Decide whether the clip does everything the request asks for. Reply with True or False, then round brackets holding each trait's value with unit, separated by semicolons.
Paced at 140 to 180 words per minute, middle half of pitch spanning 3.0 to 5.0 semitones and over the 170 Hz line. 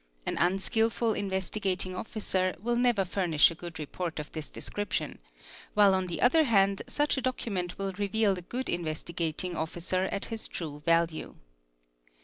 True (155 wpm; 3.9 semitones; 190 Hz)